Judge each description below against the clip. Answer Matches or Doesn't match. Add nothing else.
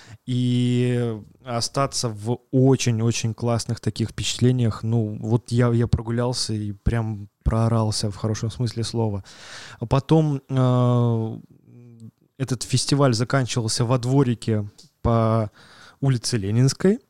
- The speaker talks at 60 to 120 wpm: Matches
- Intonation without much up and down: Matches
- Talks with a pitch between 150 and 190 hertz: Doesn't match